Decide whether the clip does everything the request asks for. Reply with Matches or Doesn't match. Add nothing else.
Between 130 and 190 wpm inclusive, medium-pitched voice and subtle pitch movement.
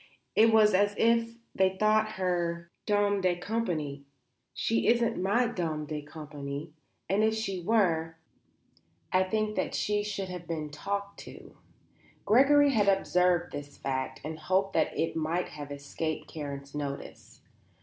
Doesn't match